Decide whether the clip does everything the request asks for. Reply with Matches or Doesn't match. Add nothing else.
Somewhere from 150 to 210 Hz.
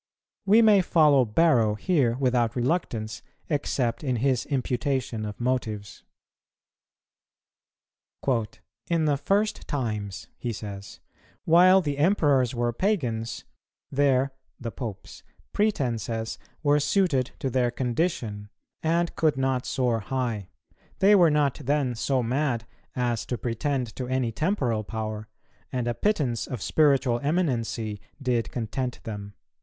Doesn't match